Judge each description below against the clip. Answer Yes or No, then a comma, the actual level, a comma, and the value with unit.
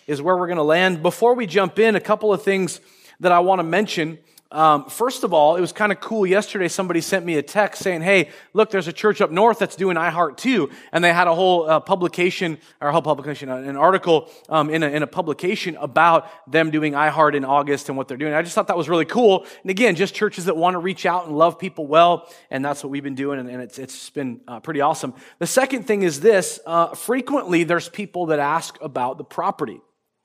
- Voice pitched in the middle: Yes, medium, 175 Hz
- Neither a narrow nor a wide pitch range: Yes, average, 4.1 semitones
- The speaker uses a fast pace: Yes, fast, 245 wpm